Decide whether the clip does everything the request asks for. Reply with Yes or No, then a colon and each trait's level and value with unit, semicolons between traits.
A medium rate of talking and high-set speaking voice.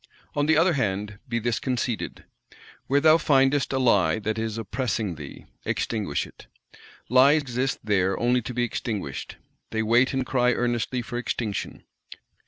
No: average, 155 wpm; low, 120 Hz